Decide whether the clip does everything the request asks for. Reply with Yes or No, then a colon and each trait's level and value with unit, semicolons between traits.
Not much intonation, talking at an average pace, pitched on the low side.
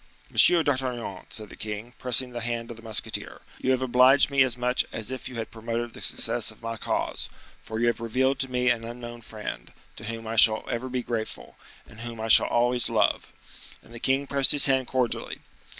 No: narrow, 2.1 semitones; fast, 215 wpm; low, 120 Hz